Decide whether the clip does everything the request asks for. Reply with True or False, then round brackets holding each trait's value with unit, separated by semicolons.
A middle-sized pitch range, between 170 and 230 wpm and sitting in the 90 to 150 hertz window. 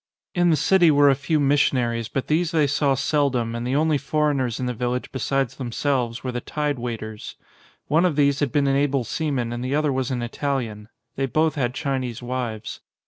True (3.1 semitones; 200 wpm; 135 Hz)